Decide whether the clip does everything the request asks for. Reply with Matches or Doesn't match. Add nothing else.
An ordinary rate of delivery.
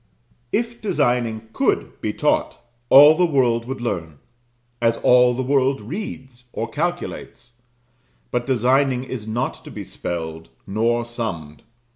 Doesn't match